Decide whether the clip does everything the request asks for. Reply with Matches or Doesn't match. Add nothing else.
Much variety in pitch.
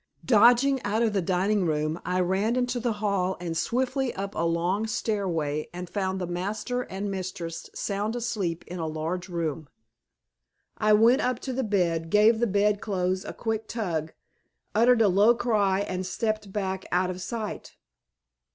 Doesn't match